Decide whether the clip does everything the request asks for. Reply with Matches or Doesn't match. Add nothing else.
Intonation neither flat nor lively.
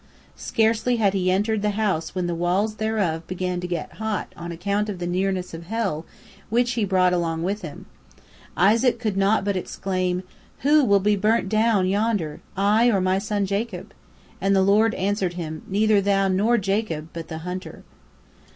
Matches